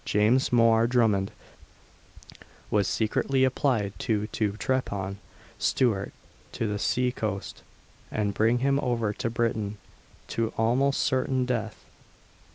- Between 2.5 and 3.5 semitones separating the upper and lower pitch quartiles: Yes, average, 3.2 semitones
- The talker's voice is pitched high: No, low, 115 Hz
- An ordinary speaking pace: No, slow, 115 wpm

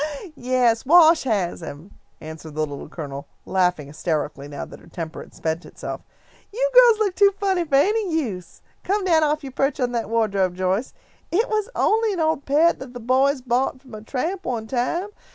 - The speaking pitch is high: Yes, very high, 255 Hz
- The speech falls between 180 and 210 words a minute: Yes, average, 190 wpm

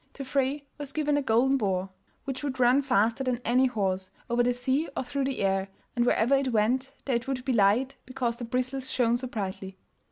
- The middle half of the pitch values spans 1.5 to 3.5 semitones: Yes, average, 2.9 semitones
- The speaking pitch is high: Yes, very high, 250 Hz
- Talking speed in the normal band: No, fast, 215 wpm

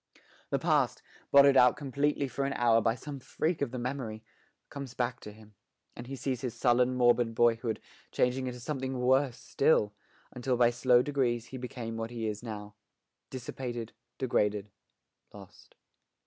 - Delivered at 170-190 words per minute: No, average, 160 wpm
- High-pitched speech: No, low, 125 Hz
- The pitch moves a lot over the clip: No, narrow, 2.5 semitones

